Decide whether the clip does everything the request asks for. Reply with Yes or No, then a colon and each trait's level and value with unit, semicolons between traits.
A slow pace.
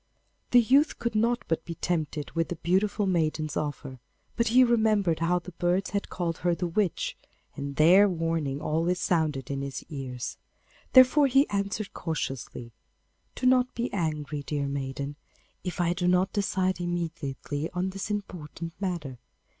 No: average, 155 wpm